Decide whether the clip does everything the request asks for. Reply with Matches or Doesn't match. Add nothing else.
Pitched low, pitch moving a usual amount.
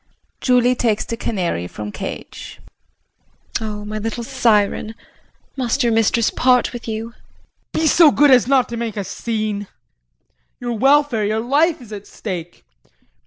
Doesn't match